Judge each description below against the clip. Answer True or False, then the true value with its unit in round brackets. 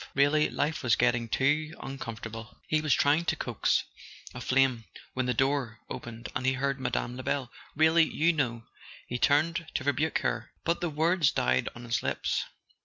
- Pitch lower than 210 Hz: True (135 Hz)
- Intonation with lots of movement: False (4.1 semitones)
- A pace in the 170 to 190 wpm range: True (185 wpm)